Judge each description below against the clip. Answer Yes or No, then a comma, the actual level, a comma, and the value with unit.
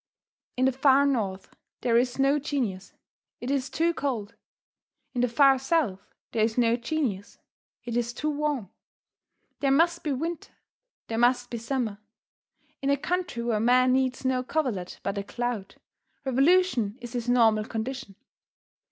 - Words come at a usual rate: Yes, average, 155 wpm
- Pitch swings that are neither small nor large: Yes, average, 3.4 semitones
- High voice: Yes, very high, 250 Hz